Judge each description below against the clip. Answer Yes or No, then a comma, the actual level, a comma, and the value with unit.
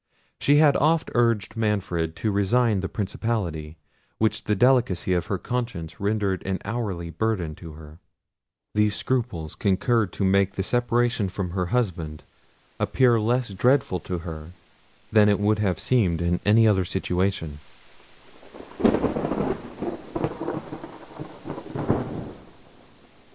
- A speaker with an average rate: No, slow, 115 wpm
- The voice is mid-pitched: No, low, 100 Hz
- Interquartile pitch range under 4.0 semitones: No, average, 4.6 semitones